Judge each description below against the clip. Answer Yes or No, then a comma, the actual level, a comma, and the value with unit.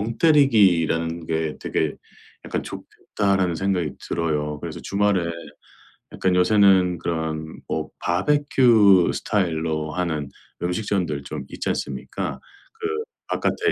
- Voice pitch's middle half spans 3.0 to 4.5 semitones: Yes, average, 4.1 semitones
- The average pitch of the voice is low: Yes, very low, 90 Hz